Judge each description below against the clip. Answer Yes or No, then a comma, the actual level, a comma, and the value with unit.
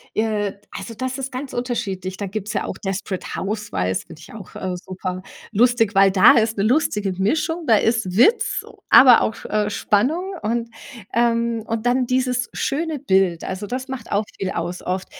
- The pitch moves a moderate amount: Yes, average, 4.2 semitones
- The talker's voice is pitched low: No, high, 215 Hz